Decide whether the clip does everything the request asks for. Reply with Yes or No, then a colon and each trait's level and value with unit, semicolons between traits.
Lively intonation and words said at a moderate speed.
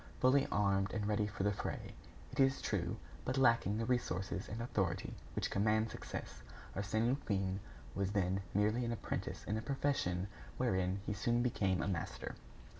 No: average, 3.3 semitones; average, 165 wpm